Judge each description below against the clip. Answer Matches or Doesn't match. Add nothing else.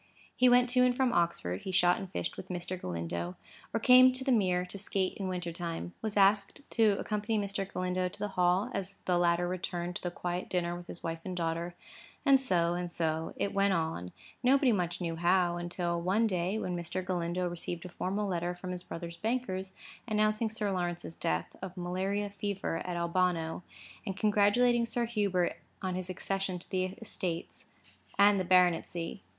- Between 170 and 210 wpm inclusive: Matches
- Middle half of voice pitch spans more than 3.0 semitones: Doesn't match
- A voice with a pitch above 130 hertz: Matches